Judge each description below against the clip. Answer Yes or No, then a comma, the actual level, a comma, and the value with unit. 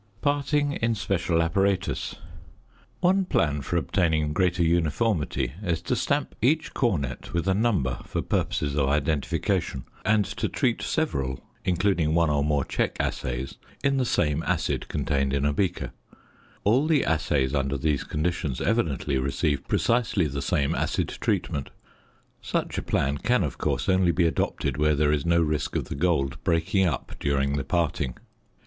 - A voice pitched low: Yes, very low, 80 Hz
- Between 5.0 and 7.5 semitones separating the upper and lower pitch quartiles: Yes, wide, 5.6 semitones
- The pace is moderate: Yes, average, 155 wpm